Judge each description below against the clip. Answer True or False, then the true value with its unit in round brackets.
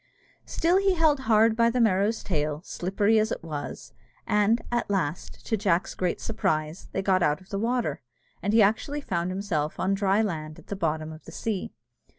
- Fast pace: False (190 wpm)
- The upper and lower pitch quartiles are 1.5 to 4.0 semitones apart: False (4.9 semitones)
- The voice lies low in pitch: False (200 Hz)